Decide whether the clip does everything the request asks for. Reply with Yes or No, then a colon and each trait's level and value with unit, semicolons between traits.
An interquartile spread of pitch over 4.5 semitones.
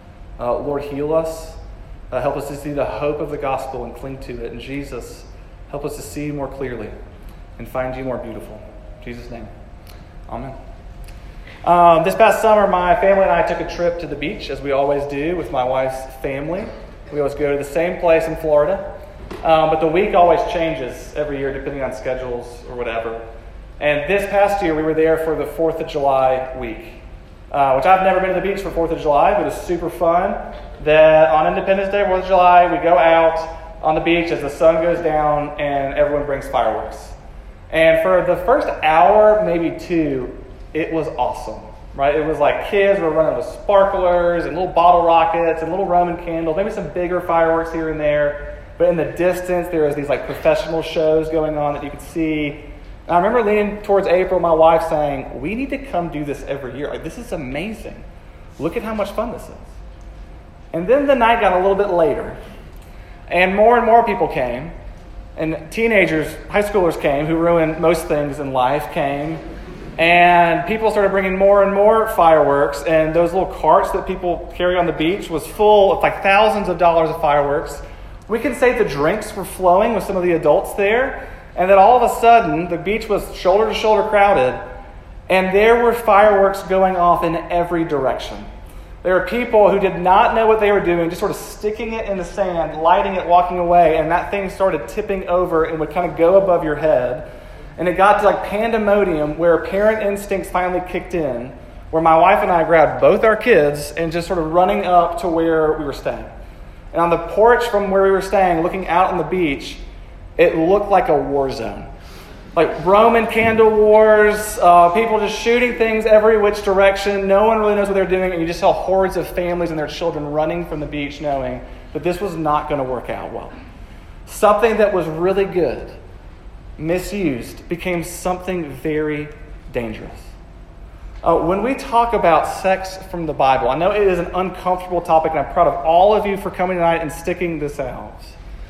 Yes: average, 5.0 semitones